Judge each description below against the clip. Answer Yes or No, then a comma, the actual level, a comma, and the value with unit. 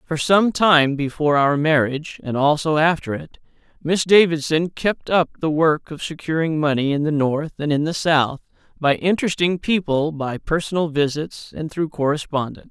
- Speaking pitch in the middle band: Yes, medium, 155 Hz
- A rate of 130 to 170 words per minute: Yes, average, 165 wpm